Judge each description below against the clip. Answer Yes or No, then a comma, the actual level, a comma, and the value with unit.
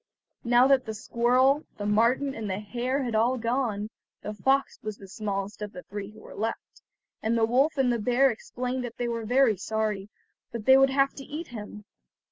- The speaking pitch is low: No, high, 235 Hz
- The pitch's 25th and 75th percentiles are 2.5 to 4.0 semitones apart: Yes, average, 3.6 semitones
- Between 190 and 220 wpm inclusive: Yes, fast, 205 wpm